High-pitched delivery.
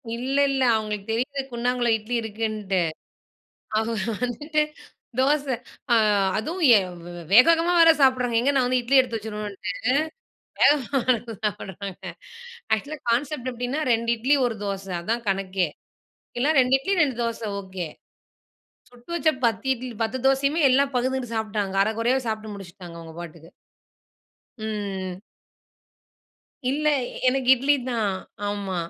Yes: high, 230 Hz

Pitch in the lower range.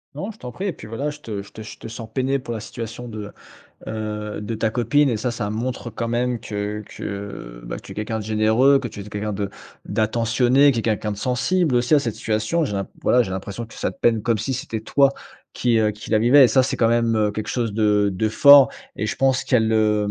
Yes: low, 115 Hz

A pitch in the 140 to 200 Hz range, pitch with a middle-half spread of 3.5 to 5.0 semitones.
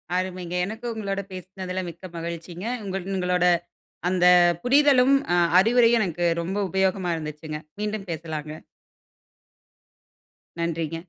No: medium, 185 Hz; average, 2.9 semitones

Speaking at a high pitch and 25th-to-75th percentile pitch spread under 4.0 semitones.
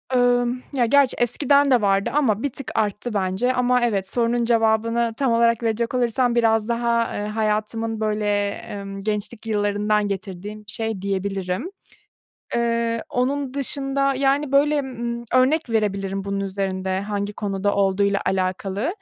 Yes: high, 225 Hz; average, 3.4 semitones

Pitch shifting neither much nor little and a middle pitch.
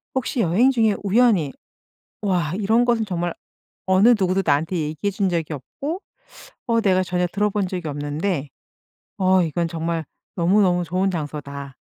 Yes: average, 3.9 semitones; medium, 180 Hz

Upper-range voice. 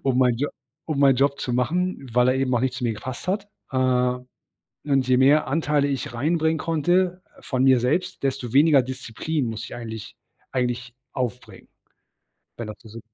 No: low, 130 Hz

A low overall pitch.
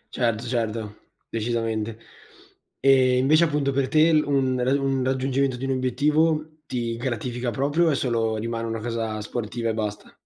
Yes: low, 125 Hz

